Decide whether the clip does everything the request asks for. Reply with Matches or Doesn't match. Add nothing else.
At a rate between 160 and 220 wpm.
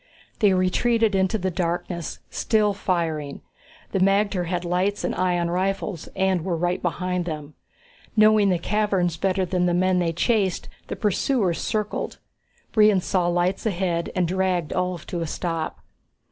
Doesn't match